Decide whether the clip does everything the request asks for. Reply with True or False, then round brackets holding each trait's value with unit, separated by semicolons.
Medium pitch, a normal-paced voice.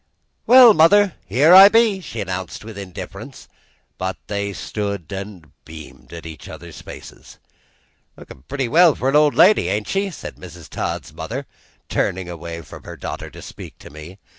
False (100 Hz; 165 wpm)